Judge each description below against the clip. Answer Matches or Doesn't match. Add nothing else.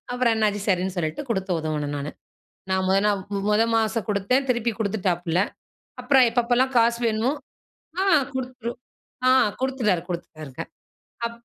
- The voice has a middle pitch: Doesn't match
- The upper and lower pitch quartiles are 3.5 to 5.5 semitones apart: Matches